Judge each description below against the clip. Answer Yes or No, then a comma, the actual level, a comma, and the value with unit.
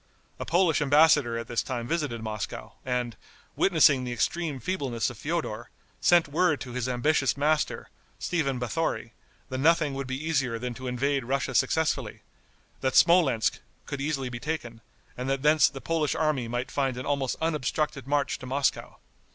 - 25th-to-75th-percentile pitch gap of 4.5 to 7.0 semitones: No, average, 3.7 semitones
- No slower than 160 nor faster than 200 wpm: Yes, average, 165 wpm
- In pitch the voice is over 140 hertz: No, low, 135 Hz